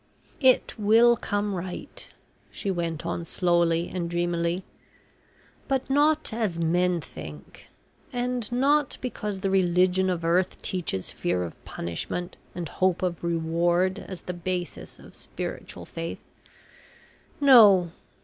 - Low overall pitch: No, medium, 180 Hz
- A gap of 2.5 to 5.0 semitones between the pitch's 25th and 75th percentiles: Yes, average, 3.6 semitones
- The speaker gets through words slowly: Yes, slow, 120 wpm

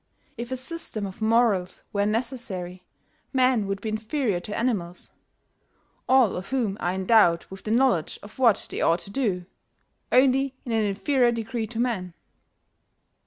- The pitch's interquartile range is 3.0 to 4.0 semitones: No, average, 4.7 semitones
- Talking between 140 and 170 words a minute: Yes, average, 155 wpm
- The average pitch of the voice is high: Yes, high, 220 Hz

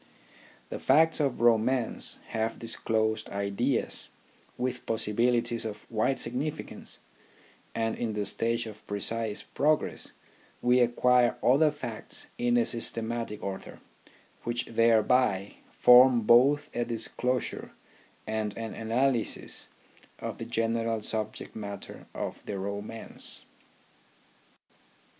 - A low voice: Yes, low, 115 Hz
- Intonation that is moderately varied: No, narrow, 2.2 semitones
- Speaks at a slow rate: Yes, slow, 105 wpm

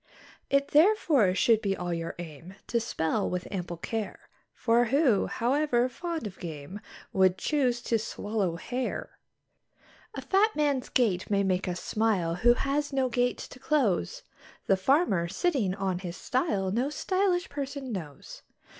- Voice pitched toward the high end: Yes, high, 225 Hz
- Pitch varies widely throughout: Yes, wide, 6.8 semitones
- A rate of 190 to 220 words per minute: No, average, 150 wpm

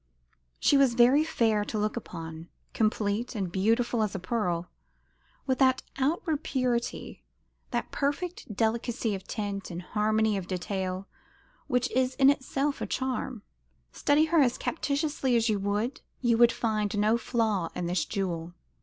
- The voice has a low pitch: No, high, 225 Hz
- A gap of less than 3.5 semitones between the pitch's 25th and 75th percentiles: No, average, 4.5 semitones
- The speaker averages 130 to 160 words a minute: Yes, average, 150 wpm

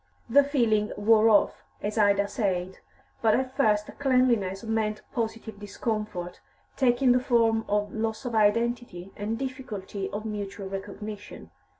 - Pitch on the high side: Yes, high, 215 Hz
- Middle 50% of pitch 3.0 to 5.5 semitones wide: No, narrow, 2.6 semitones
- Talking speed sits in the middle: No, slow, 130 wpm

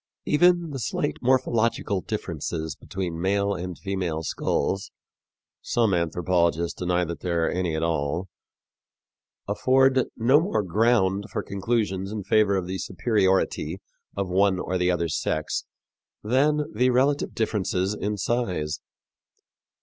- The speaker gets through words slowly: Yes, slow, 125 wpm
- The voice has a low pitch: Yes, very low, 95 Hz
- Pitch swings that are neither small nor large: Yes, average, 4.7 semitones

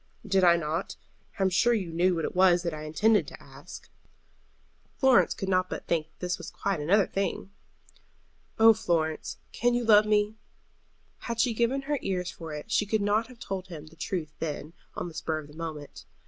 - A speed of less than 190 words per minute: No, fast, 205 wpm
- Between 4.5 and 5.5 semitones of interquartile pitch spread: Yes, average, 4.8 semitones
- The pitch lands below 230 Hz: Yes, medium, 185 Hz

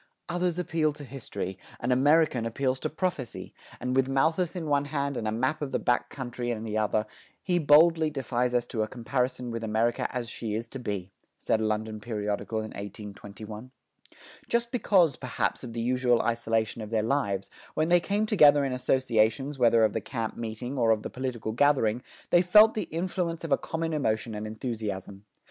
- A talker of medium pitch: No, low, 125 Hz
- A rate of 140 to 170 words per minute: No, average, 190 wpm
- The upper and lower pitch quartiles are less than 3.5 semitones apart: No, average, 5.1 semitones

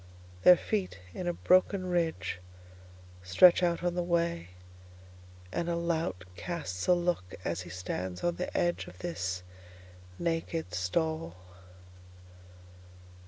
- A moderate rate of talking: No, slow, 115 wpm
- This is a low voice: No, medium, 160 Hz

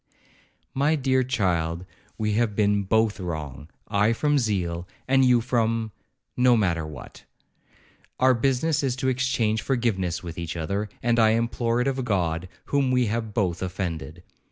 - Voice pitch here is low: Yes, low, 110 Hz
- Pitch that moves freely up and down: Yes, wide, 5.7 semitones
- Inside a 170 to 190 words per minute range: No, average, 150 wpm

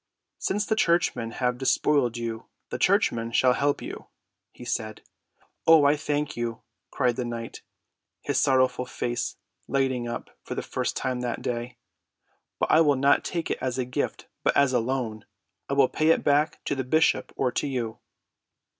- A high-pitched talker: No, low, 130 Hz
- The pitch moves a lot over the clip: No, average, 3.2 semitones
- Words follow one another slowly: No, average, 175 wpm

